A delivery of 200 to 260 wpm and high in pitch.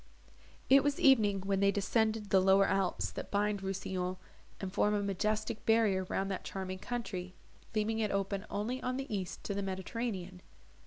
No: average, 170 wpm; high, 200 Hz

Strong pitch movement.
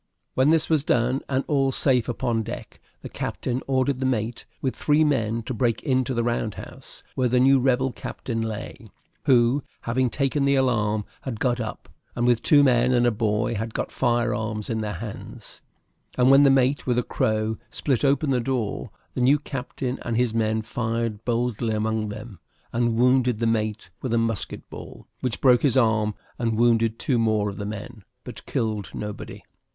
No: average, 2.8 semitones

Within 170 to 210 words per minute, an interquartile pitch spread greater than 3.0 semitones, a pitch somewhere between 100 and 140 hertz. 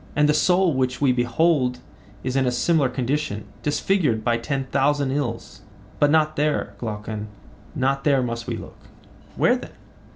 No: average, 160 wpm; average, 3.4 semitones; low, 135 Hz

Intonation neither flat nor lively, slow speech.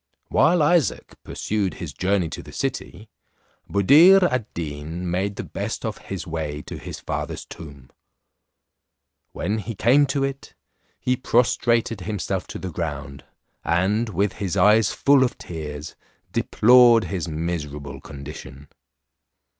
No: wide, 6.6 semitones; slow, 130 wpm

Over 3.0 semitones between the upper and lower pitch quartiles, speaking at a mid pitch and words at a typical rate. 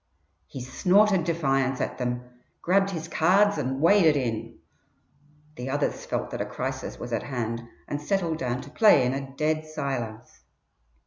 Yes: average, 5.0 semitones; medium, 145 Hz; average, 155 wpm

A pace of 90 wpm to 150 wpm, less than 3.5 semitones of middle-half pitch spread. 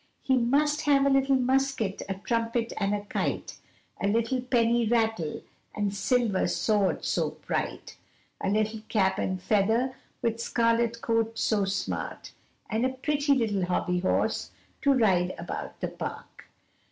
No: average, 145 wpm; average, 4.0 semitones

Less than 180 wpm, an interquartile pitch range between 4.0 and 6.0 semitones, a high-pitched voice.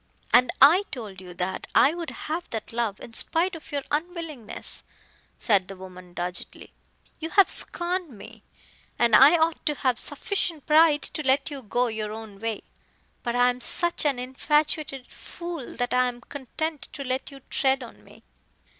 Yes: average, 170 wpm; wide, 5.4 semitones; very high, 265 Hz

